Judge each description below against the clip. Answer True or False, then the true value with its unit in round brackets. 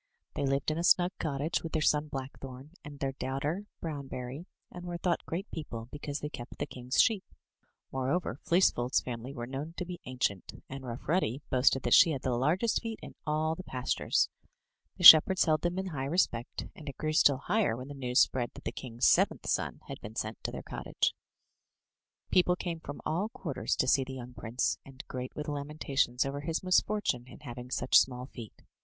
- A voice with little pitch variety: False (4.3 semitones)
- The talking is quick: True (210 wpm)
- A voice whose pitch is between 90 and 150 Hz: True (140 Hz)